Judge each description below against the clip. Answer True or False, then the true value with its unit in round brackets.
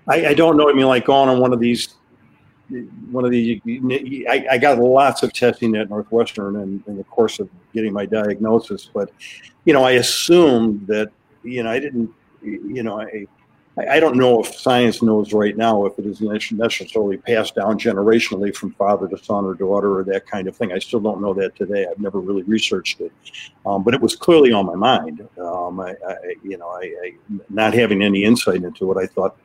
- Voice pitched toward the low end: True (110 Hz)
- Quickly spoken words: True (215 wpm)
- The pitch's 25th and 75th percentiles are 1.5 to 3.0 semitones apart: False (3.5 semitones)